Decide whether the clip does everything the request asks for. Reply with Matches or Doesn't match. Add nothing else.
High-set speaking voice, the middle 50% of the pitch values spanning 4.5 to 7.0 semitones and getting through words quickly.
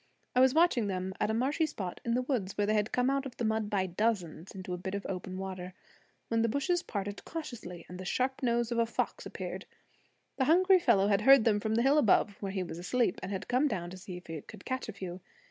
Matches